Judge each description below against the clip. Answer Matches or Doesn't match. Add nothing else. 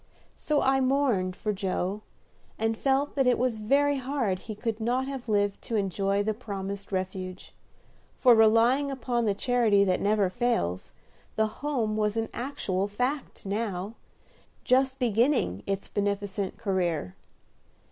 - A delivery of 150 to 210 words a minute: Doesn't match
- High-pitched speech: Matches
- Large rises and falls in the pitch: Doesn't match